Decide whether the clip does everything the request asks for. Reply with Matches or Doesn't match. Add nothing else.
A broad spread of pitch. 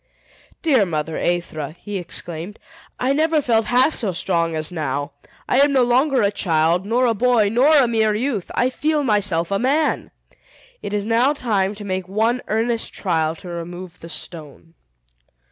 Matches